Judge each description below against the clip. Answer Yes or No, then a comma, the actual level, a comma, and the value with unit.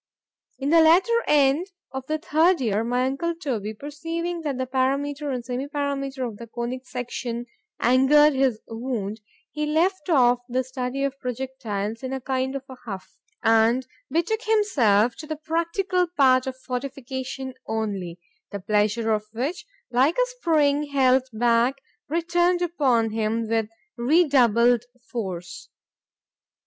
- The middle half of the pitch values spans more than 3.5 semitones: Yes, average, 4.3 semitones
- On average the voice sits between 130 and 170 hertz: No, very high, 260 Hz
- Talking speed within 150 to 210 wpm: No, average, 140 wpm